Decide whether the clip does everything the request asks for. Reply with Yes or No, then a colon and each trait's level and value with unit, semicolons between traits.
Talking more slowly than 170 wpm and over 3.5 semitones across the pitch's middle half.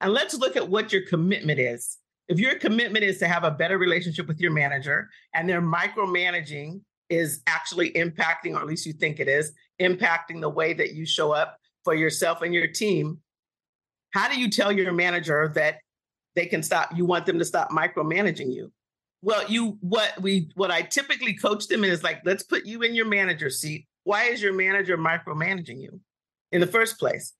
No: average, 195 wpm; average, 3.9 semitones